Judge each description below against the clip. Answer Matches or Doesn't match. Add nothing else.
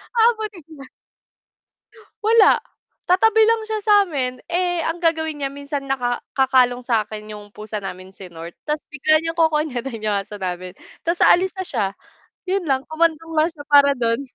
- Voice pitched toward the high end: Matches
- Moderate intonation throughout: Doesn't match